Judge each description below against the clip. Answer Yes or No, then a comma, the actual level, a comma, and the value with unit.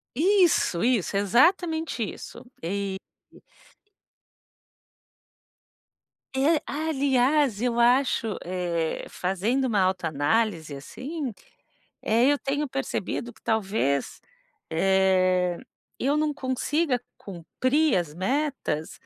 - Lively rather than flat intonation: Yes, wide, 7.3 semitones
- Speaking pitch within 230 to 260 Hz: Yes, high, 235 Hz